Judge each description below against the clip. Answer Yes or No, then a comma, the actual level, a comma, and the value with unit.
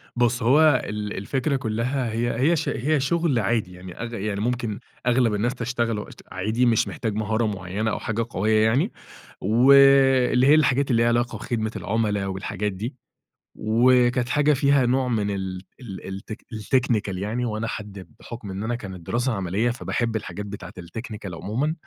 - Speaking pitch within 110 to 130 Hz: Yes, low, 115 Hz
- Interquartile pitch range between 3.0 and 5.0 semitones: Yes, average, 3.3 semitones